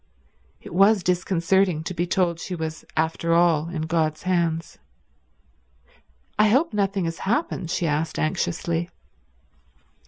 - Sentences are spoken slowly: Yes, slow, 125 wpm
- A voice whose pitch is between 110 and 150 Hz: No, medium, 170 Hz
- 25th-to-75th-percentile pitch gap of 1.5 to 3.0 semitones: Yes, average, 2.7 semitones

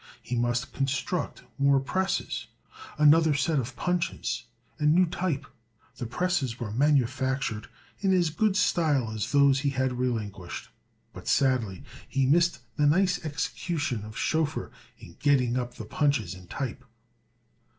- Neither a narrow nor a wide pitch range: Yes, average, 4.7 semitones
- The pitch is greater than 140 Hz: No, low, 135 Hz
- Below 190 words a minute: Yes, average, 140 wpm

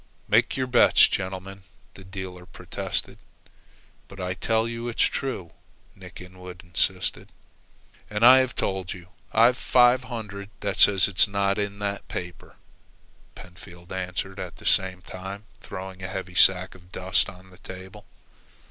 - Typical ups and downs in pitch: No, narrow, 2.0 semitones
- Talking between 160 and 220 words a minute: No, average, 150 wpm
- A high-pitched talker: No, very low, 95 Hz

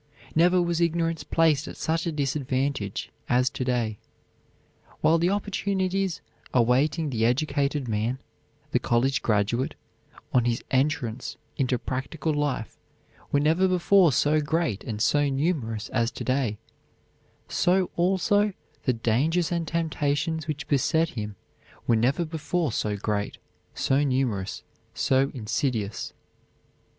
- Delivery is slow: Yes, slow, 125 wpm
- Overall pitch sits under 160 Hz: Yes, medium, 140 Hz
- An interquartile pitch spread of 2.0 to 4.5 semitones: No, average, 5.3 semitones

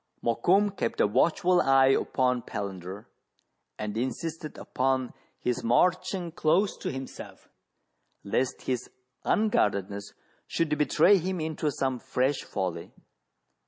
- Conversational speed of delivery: No, slow, 110 wpm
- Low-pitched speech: Yes, low, 130 Hz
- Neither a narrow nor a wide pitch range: No, wide, 6.1 semitones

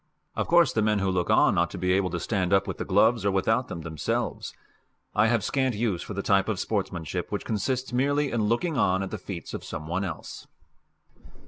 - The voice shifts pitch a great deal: No, average, 4.1 semitones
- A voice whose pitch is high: No, low, 100 Hz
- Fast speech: Yes, fast, 225 wpm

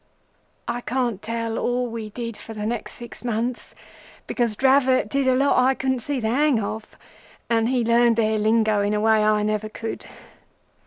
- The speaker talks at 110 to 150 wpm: No, average, 180 wpm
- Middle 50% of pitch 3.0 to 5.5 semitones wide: No, narrow, 2.5 semitones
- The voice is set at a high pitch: Yes, high, 230 Hz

